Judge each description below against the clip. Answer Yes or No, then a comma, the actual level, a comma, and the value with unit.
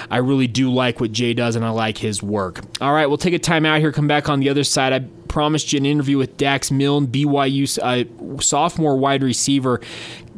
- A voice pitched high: No, low, 135 Hz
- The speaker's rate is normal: No, fast, 220 wpm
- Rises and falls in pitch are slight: No, average, 3.2 semitones